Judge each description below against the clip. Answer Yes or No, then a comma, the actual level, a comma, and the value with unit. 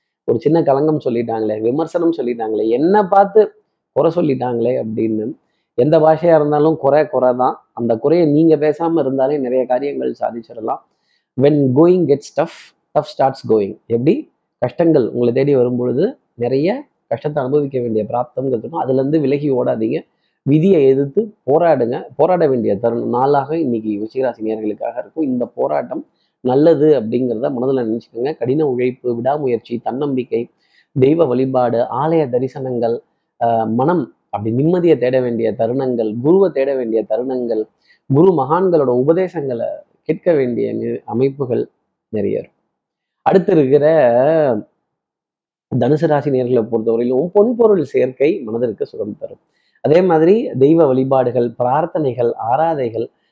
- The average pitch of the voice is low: Yes, low, 130 Hz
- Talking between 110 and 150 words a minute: Yes, average, 115 wpm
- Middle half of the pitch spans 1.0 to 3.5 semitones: No, average, 4.7 semitones